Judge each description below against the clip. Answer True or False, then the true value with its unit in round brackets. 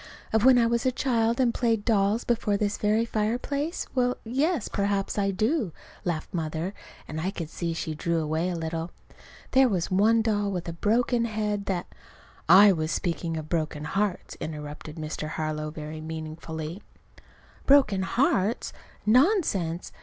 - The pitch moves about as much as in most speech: False (6.0 semitones)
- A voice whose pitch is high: True (200 Hz)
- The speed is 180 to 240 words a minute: False (160 wpm)